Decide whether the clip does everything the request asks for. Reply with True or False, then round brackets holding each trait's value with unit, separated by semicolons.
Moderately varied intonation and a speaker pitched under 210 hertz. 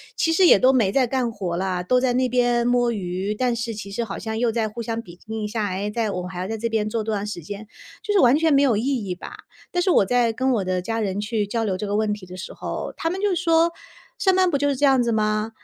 False (3.7 semitones; 225 Hz)